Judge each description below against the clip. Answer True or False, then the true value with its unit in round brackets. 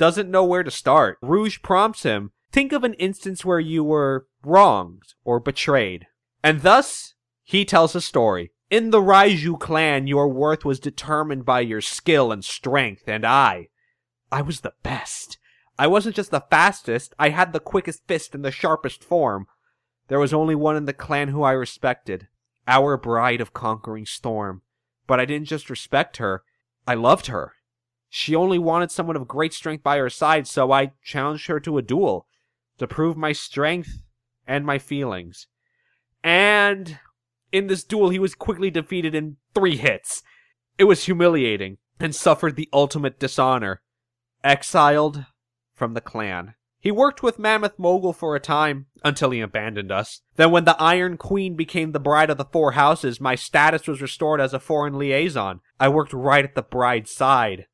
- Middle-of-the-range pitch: True (145 Hz)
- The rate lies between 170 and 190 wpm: True (175 wpm)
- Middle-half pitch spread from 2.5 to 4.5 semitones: False (5.0 semitones)